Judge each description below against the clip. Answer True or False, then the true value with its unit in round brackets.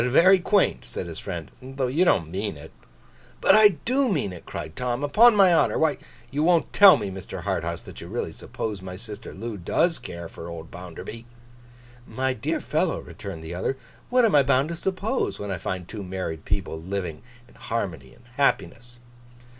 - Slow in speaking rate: False (190 wpm)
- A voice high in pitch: False (115 Hz)